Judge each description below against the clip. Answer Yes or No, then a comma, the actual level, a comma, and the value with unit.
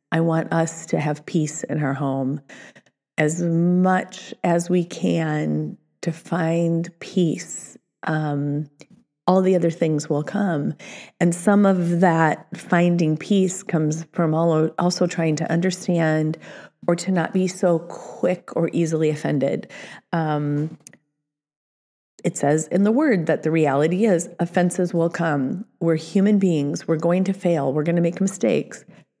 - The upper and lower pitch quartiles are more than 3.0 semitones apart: No, narrow, 2.6 semitones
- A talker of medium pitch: Yes, medium, 165 Hz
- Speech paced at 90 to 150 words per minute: Yes, average, 145 wpm